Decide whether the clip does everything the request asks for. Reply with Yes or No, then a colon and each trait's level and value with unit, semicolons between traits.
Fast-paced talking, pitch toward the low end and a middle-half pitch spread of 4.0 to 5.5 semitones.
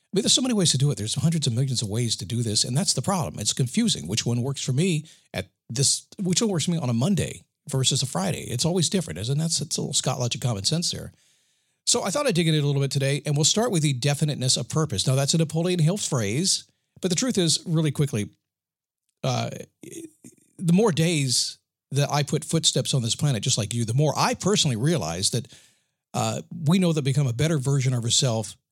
No: fast, 245 wpm; medium, 145 Hz; average, 4.5 semitones